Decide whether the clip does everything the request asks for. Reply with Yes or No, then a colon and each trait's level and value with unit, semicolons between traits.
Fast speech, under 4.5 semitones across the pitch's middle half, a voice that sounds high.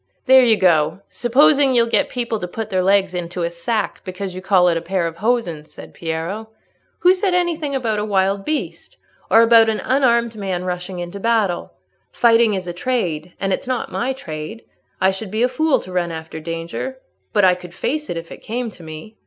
No: fast, 210 wpm; average, 5.1 semitones; high, 200 Hz